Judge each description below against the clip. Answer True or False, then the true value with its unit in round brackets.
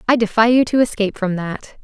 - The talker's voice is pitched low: False (220 Hz)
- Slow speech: False (230 wpm)